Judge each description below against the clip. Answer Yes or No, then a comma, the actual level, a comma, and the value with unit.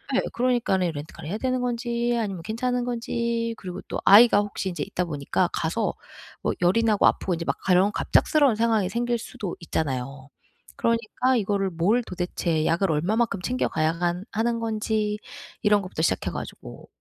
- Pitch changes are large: No, average, 4.9 semitones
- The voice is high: Yes, high, 210 Hz